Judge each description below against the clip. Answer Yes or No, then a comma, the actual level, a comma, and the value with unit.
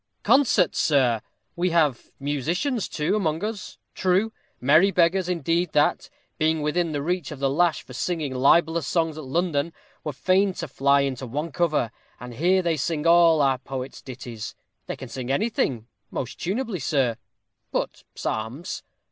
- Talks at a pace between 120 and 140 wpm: No, average, 160 wpm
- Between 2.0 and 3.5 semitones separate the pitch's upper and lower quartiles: No, average, 4.5 semitones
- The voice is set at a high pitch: No, medium, 155 Hz